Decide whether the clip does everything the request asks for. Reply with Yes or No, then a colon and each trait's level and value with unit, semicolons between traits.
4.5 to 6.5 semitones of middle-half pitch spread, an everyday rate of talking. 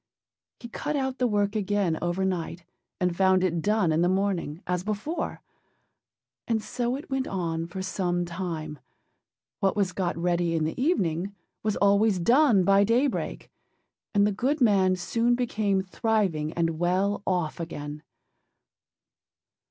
No: average, 3.8 semitones; average, 145 wpm